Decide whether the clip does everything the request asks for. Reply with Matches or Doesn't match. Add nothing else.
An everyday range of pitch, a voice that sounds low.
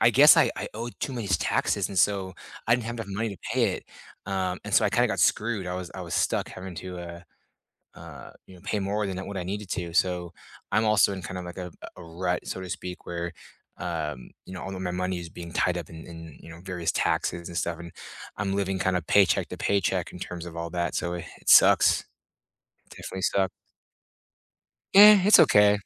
Doesn't match